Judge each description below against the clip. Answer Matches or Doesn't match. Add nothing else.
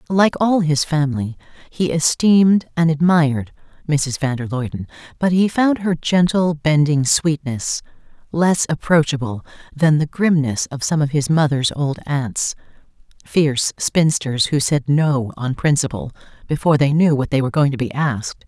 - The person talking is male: Doesn't match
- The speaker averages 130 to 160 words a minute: Matches